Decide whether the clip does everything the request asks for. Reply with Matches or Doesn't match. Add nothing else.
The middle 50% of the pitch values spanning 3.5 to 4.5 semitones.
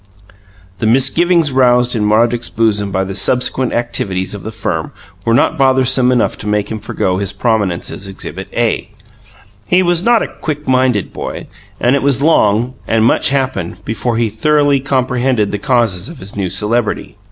Matches